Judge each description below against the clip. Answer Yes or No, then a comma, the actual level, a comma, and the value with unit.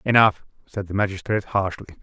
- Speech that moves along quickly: No, average, 150 wpm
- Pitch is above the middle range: No, low, 100 Hz